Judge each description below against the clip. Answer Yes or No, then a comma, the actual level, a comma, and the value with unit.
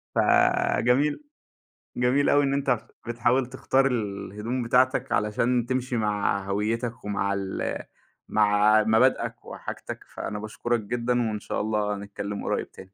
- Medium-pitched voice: No, low, 115 Hz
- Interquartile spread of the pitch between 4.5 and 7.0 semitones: No, average, 3.3 semitones